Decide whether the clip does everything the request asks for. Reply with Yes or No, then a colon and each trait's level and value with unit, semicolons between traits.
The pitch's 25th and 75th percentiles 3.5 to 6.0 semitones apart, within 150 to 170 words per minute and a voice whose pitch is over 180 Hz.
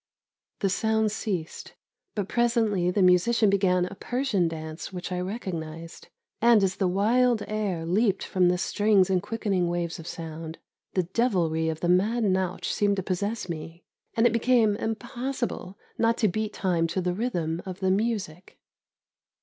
Yes: average, 3.8 semitones; average, 160 wpm; high, 190 Hz